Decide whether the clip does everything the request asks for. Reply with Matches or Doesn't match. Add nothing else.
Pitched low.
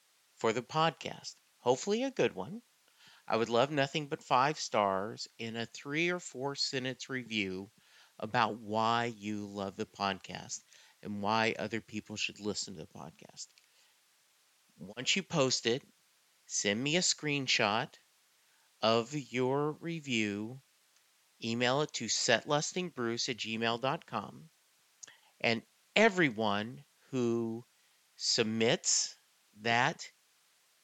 Matches